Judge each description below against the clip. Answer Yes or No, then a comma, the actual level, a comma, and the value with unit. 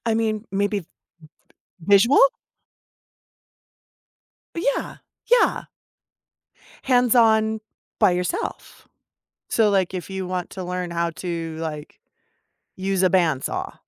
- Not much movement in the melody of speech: No, average, 3.7 semitones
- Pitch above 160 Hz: Yes, high, 190 Hz